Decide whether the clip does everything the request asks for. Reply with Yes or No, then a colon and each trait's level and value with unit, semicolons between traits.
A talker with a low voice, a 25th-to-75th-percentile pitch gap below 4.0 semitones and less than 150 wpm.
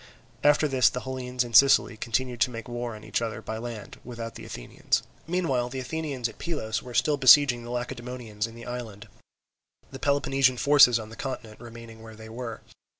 No: low, 120 Hz; narrow, 2.4 semitones; average, 190 wpm